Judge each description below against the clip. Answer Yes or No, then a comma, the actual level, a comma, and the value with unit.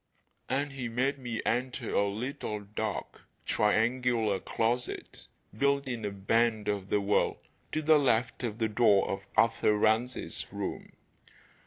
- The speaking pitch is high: No, low, 115 Hz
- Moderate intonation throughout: Yes, average, 3.2 semitones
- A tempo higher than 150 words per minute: No, average, 140 wpm